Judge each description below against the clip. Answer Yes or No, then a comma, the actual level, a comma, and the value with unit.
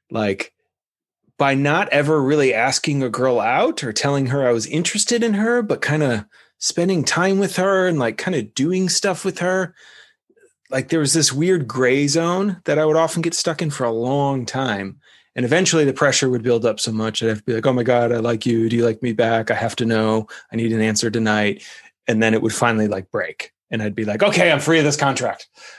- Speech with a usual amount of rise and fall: No, wide, 6.5 semitones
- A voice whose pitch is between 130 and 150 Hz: Yes, medium, 140 Hz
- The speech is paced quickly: Yes, fast, 235 wpm